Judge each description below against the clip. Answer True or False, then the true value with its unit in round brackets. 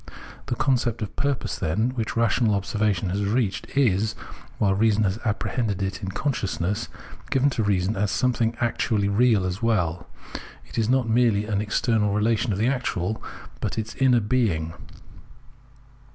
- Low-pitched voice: True (110 Hz)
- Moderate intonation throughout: True (3.0 semitones)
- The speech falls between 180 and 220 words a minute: False (150 wpm)